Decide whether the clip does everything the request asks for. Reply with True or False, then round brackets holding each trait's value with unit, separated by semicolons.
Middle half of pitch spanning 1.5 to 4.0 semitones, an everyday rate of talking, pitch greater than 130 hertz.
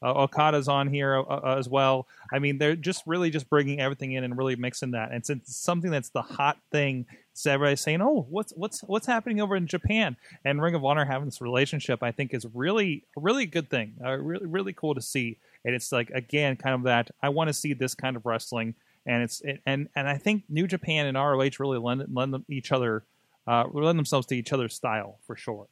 False (3.5 semitones; 235 wpm; 140 Hz)